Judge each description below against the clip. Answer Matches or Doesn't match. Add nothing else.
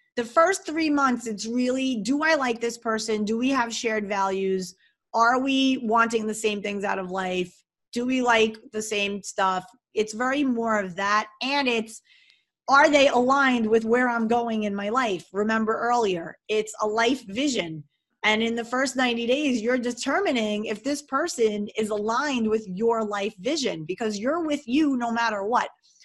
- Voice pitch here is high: Matches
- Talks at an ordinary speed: Matches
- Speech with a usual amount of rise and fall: Matches